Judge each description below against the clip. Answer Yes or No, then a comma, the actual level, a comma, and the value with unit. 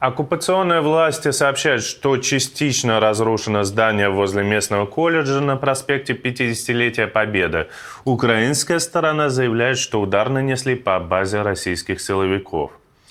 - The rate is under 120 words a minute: Yes, slow, 110 wpm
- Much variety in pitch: No, average, 4.6 semitones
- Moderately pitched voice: No, low, 125 Hz